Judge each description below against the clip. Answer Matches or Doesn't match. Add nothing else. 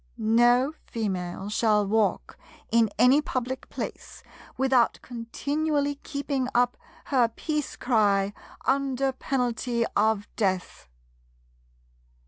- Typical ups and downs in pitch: Matches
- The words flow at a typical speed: Doesn't match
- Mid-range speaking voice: Doesn't match